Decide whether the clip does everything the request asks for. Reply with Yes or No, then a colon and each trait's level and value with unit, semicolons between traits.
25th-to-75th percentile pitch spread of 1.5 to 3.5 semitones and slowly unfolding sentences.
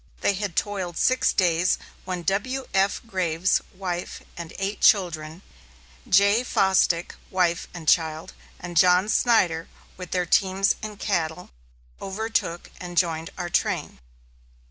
Yes: narrow, 2.5 semitones; slow, 120 wpm